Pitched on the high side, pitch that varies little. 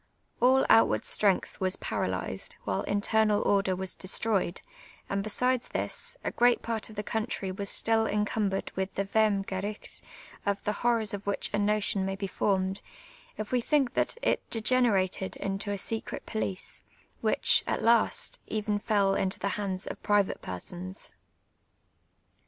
Yes: high, 205 Hz; narrow, 2.3 semitones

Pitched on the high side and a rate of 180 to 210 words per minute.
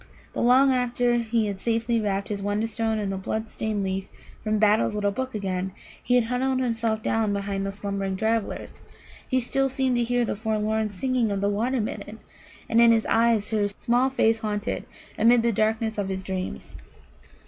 Yes: high, 220 Hz; average, 185 wpm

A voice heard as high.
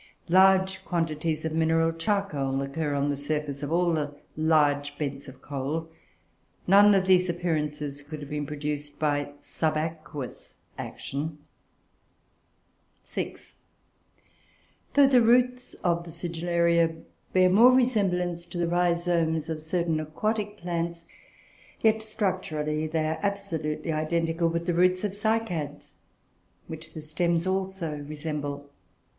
No: medium, 165 Hz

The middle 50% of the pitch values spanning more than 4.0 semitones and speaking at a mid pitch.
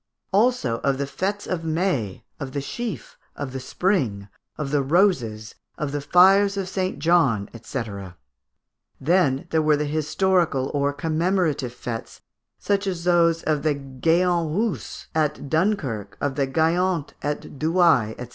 Yes: average, 5.0 semitones; medium, 155 Hz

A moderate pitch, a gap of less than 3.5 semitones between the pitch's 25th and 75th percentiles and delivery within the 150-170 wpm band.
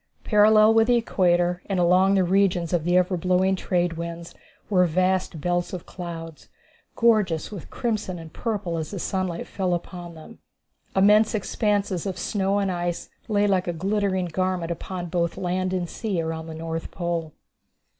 Yes: medium, 180 Hz; narrow, 2.5 semitones; average, 165 wpm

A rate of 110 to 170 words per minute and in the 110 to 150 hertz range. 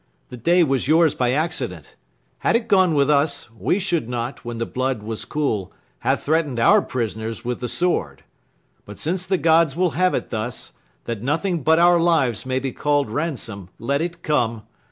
No: average, 185 wpm; medium, 140 Hz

